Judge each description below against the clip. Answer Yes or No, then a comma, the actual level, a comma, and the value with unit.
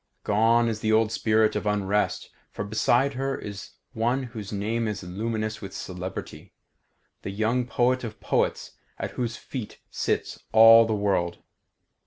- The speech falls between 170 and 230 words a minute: No, average, 150 wpm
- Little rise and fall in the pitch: Yes, narrow, 2.3 semitones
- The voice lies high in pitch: No, low, 110 Hz